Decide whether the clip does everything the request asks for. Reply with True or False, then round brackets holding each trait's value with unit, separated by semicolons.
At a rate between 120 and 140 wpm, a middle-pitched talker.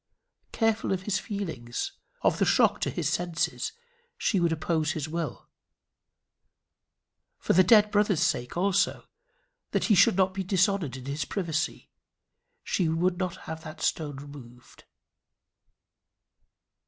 True (135 wpm; 170 Hz)